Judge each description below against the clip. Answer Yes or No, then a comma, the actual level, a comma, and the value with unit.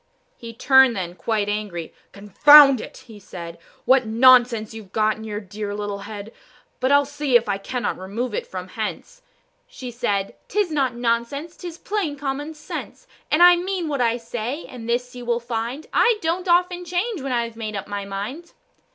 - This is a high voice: Yes, high, 240 Hz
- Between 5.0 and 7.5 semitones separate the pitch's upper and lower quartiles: Yes, wide, 5.5 semitones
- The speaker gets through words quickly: No, average, 185 wpm